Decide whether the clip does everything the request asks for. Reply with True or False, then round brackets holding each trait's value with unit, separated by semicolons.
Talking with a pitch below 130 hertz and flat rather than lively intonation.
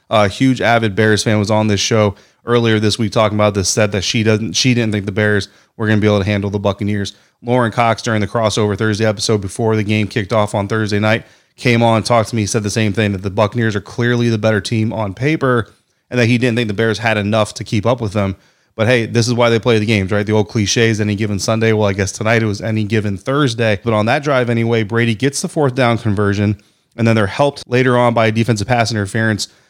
True (110 Hz; 1.9 semitones)